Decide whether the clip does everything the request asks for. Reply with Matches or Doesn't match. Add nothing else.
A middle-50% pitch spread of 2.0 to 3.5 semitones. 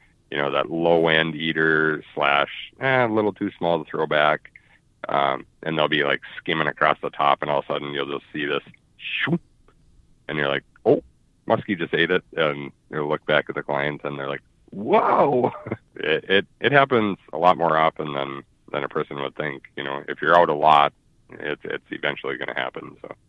Matches